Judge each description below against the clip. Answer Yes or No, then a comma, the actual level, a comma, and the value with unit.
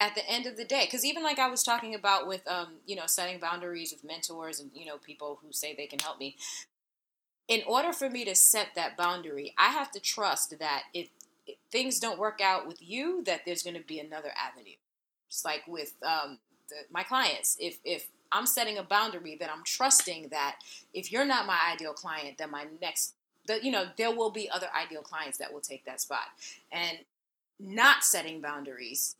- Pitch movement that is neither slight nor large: No, wide, 6.8 semitones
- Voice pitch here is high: No, medium, 175 Hz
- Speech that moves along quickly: Yes, fast, 210 wpm